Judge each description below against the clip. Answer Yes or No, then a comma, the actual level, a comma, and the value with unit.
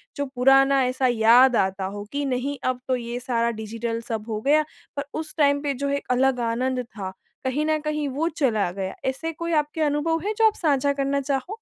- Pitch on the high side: Yes, very high, 265 Hz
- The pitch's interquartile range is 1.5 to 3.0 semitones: No, average, 3.5 semitones